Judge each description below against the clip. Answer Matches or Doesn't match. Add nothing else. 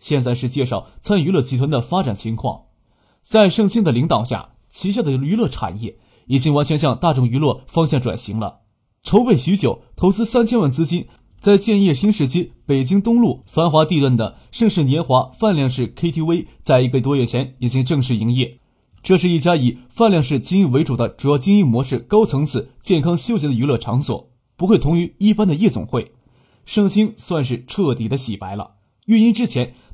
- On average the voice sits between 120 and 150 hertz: Matches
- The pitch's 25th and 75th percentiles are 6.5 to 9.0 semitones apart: Matches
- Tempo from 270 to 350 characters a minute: Matches